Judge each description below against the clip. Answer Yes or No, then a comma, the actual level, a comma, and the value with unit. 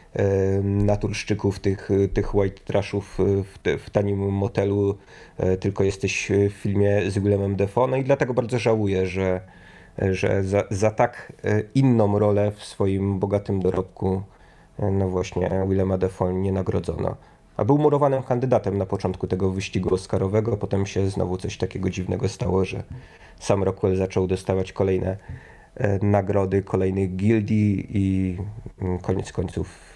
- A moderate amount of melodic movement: No, narrow, 1.6 semitones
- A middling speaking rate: Yes, average, 135 wpm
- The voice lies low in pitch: Yes, low, 100 Hz